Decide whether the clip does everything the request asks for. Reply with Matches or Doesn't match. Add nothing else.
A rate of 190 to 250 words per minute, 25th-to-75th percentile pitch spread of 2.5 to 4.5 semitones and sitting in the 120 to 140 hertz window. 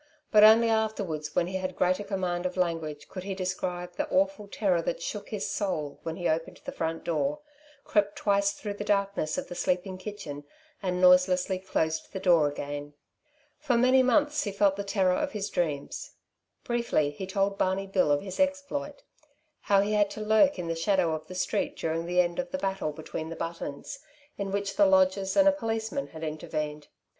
Doesn't match